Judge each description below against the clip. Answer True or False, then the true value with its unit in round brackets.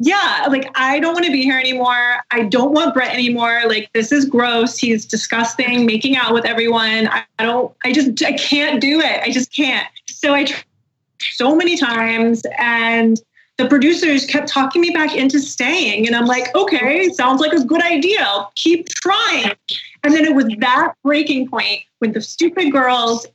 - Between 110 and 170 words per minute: False (190 wpm)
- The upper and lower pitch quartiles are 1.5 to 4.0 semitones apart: False (4.4 semitones)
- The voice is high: True (260 Hz)